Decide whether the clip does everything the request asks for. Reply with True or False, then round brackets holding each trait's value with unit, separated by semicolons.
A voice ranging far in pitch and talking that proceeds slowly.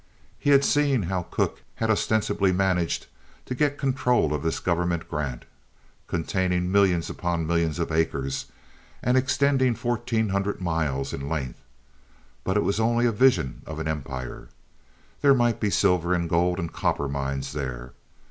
False (6.3 semitones; 150 wpm)